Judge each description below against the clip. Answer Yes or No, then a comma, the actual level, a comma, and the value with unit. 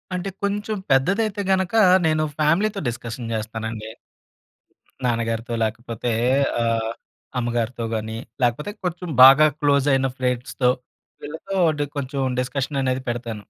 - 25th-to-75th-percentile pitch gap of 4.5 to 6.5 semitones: Yes, average, 5.1 semitones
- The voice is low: Yes, low, 130 Hz